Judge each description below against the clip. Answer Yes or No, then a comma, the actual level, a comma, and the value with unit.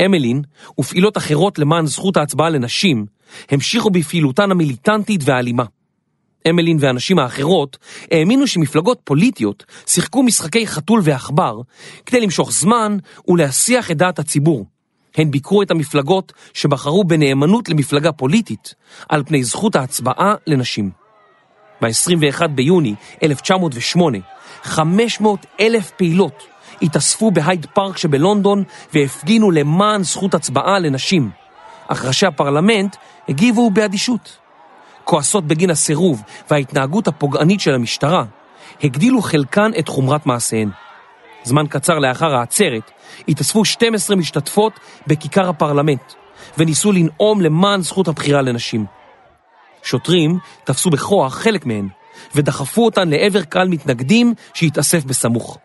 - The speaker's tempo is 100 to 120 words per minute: Yes, average, 110 wpm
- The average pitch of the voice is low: No, medium, 165 Hz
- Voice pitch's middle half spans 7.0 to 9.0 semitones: No, wide, 5.6 semitones